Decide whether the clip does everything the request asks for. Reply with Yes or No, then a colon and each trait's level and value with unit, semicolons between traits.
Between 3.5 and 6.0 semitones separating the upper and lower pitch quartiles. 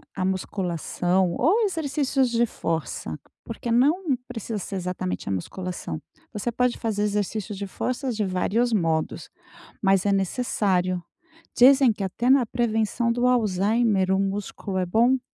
Yes: average, 4.6 semitones